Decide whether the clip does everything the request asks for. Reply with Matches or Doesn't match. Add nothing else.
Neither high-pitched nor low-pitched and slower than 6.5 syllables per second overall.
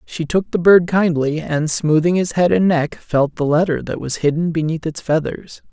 Matches